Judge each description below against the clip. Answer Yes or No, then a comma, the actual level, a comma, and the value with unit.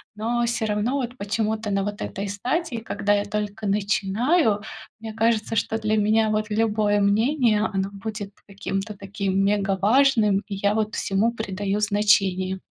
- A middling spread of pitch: No, narrow, 1.8 semitones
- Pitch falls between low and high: No, high, 210 Hz